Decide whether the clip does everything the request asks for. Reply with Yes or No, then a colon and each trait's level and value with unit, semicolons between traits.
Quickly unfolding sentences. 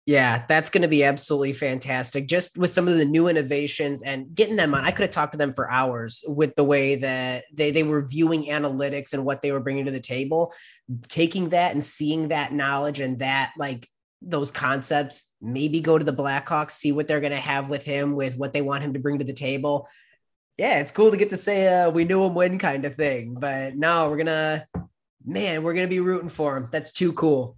Yes: fast, 235 wpm